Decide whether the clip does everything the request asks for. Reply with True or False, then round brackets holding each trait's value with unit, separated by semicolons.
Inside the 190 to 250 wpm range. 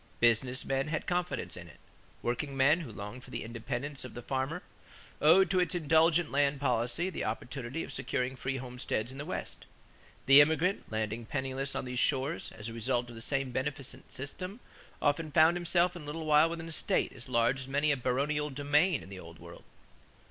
True (195 wpm)